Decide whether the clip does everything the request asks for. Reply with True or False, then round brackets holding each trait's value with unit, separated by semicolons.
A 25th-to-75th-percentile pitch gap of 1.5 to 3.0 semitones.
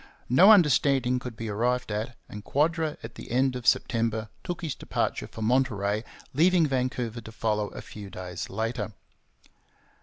False (3.7 semitones)